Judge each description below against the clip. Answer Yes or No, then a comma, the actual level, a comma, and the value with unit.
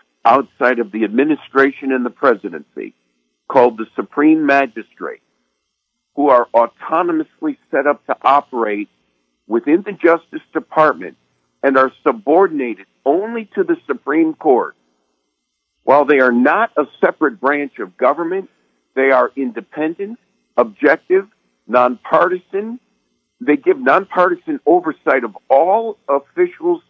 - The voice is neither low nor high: Yes, medium, 145 Hz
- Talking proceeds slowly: Yes, slow, 115 wpm